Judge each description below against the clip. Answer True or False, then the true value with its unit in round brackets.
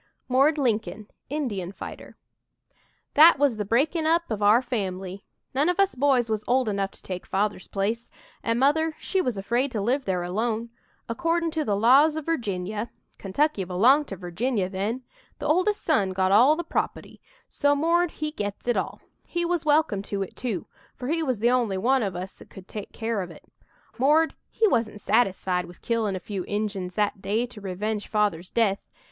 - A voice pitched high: True (230 Hz)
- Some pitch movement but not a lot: False (6.5 semitones)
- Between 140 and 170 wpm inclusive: False (190 wpm)